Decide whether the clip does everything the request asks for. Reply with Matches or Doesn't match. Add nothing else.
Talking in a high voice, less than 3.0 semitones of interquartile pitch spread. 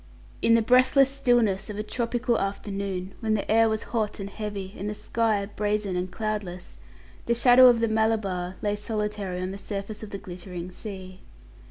Matches